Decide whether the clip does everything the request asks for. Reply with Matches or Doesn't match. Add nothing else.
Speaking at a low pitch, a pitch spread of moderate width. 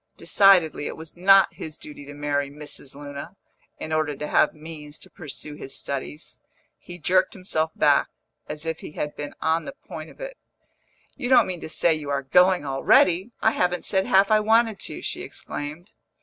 Doesn't match